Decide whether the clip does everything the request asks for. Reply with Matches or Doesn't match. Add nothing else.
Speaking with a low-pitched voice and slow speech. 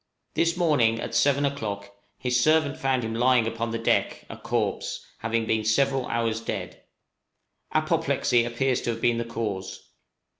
Doesn't match